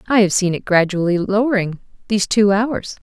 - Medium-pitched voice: No, high, 200 Hz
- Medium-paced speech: Yes, average, 155 wpm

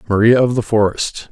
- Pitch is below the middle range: Yes, low, 110 Hz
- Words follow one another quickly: No, average, 185 wpm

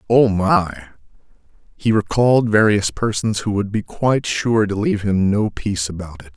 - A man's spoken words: Yes, male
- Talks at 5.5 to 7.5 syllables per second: No, 5.0 syllables/s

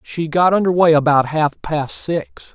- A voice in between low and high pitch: Yes, medium, 150 Hz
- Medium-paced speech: Yes, average, 190 wpm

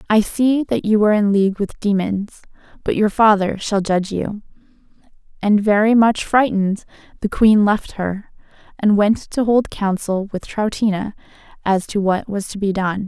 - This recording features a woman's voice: Yes, female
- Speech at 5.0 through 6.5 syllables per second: No, 4.8 syllables/s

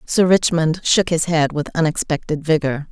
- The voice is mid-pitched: Yes, medium, 160 Hz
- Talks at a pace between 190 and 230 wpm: No, average, 165 wpm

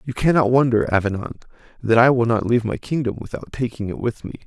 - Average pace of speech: No, fast, 215 wpm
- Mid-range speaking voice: No, low, 120 Hz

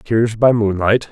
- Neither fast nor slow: Yes, average, 160 wpm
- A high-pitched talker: No, low, 110 Hz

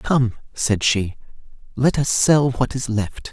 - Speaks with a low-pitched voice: Yes, low, 125 Hz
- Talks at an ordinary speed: Yes, average, 165 wpm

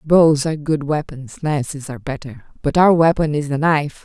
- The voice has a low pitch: No, medium, 150 Hz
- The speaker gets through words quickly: No, average, 195 wpm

